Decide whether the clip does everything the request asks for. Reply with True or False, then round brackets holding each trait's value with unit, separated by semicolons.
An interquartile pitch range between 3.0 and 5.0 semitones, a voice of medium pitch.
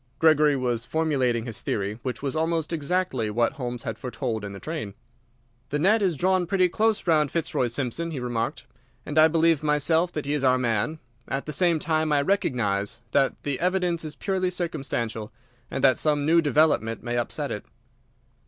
False (5.4 semitones; 150 Hz)